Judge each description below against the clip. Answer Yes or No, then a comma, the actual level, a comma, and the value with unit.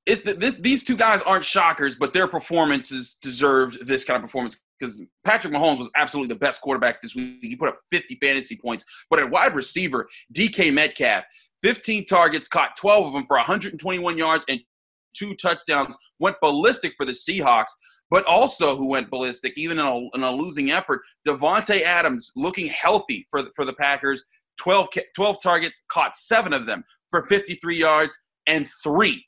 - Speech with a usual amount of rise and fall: No, wide, 6.5 semitones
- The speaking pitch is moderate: Yes, medium, 170 Hz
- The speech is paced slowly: No, average, 180 wpm